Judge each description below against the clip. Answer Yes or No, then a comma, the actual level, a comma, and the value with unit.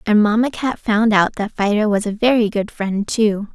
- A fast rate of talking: Yes, fast, 220 wpm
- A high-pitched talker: Yes, high, 215 Hz